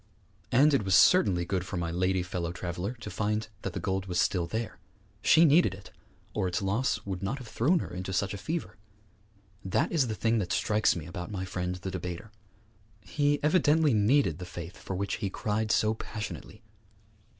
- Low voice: Yes, low, 100 Hz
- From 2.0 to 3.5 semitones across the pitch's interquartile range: No, average, 4.0 semitones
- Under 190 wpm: No, average, 195 wpm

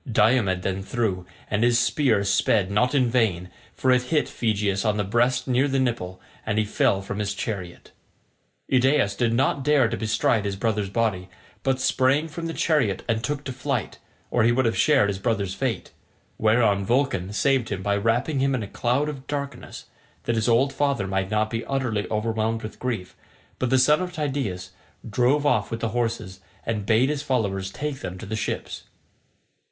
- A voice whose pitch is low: Yes, low, 115 Hz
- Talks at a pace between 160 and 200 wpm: Yes, average, 190 wpm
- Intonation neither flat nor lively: Yes, average, 4.4 semitones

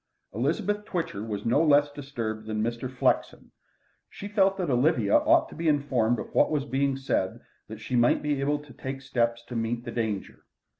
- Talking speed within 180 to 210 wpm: Yes, average, 190 wpm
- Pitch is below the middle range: Yes, low, 130 Hz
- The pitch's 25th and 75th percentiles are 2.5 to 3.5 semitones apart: No, average, 4.2 semitones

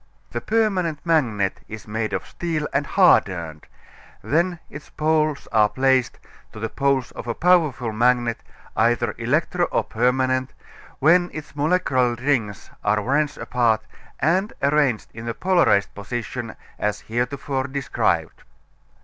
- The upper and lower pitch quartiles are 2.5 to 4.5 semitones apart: No, average, 5.1 semitones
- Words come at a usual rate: No, slow, 130 wpm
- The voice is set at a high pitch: No, low, 130 Hz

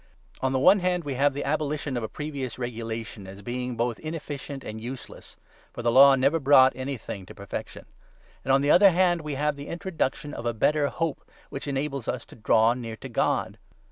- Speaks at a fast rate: Yes, fast, 210 wpm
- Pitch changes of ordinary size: Yes, average, 3.9 semitones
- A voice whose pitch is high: No, low, 135 Hz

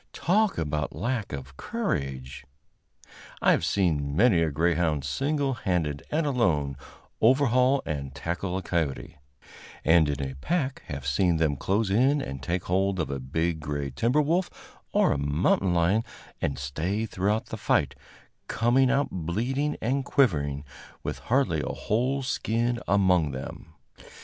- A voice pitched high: No, very low, 90 Hz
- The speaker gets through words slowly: No, average, 150 wpm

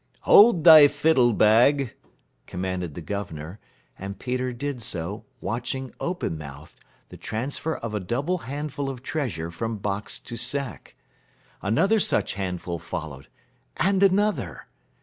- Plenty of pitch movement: Yes, wide, 7.2 semitones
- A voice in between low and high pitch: No, low, 120 Hz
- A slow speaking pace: Yes, slow, 130 wpm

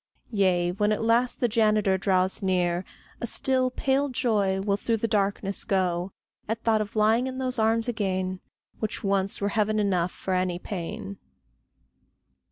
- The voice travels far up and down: No, average, 3.3 semitones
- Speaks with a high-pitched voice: Yes, high, 205 Hz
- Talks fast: No, average, 160 wpm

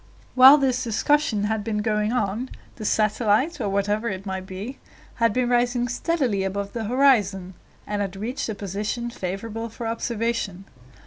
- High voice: Yes, high, 220 Hz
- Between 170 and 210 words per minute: No, average, 155 wpm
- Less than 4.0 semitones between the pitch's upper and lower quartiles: Yes, average, 3.3 semitones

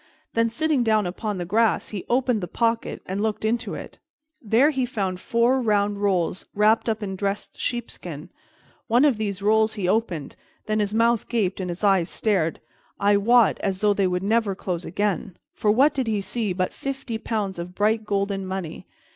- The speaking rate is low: No, average, 190 wpm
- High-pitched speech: Yes, high, 210 Hz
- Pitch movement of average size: Yes, average, 3.0 semitones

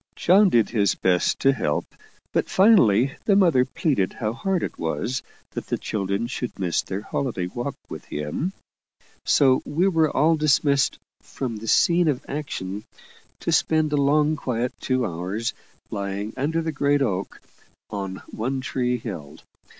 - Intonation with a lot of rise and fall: Yes, wide, 6.9 semitones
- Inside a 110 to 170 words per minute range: Yes, average, 155 wpm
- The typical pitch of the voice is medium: No, low, 125 Hz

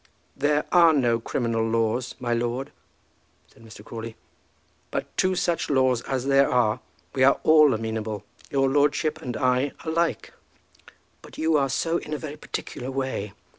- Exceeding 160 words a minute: No, average, 155 wpm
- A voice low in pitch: Yes, low, 130 Hz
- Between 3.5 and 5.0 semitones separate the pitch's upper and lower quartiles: Yes, average, 4.2 semitones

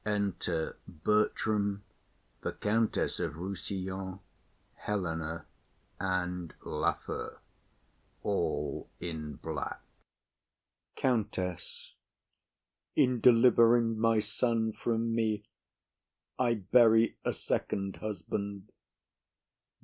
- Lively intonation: No, average, 3.7 semitones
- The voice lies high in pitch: No, low, 105 Hz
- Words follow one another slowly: Yes, slow, 75 wpm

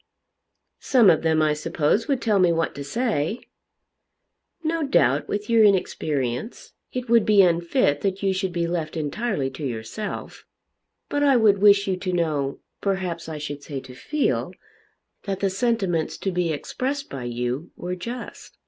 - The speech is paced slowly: No, average, 165 wpm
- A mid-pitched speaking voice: Yes, medium, 180 Hz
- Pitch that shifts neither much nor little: No, wide, 6.0 semitones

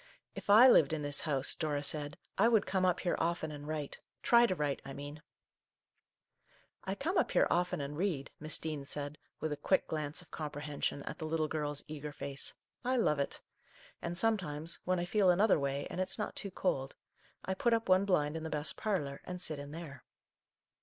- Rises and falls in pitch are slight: No, average, 4.2 semitones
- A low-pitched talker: No, medium, 155 Hz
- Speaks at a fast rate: Yes, fast, 220 wpm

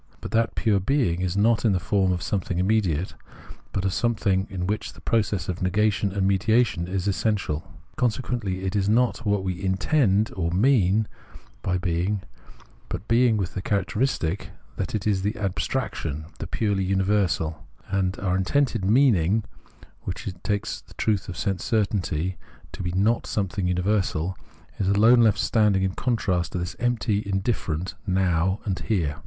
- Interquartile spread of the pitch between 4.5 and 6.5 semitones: No, average, 2.9 semitones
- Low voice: Yes, low, 100 Hz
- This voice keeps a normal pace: Yes, average, 170 wpm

